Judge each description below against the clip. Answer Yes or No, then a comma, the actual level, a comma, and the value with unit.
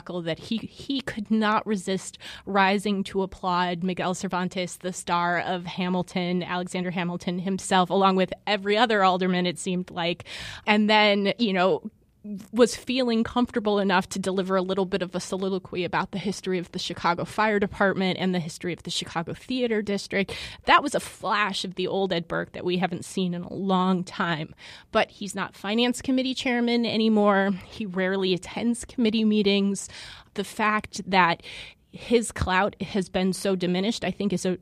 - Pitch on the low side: No, high, 190 Hz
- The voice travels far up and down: No, narrow, 2.6 semitones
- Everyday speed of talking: Yes, average, 175 wpm